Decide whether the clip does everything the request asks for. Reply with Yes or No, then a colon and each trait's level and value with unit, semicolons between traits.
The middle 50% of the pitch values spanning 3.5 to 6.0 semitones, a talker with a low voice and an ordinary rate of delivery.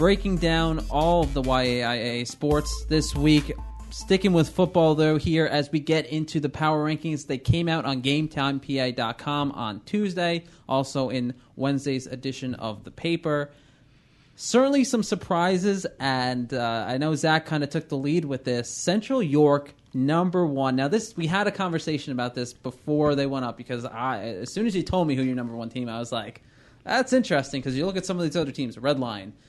No: average, 4.2 semitones; medium, 145 Hz; average, 195 wpm